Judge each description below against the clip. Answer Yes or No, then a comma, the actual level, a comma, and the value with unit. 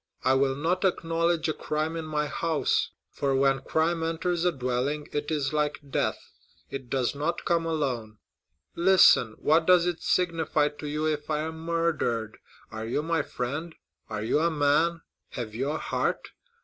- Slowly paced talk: No, average, 165 wpm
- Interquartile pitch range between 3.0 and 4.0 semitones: Yes, average, 3.4 semitones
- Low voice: No, medium, 150 Hz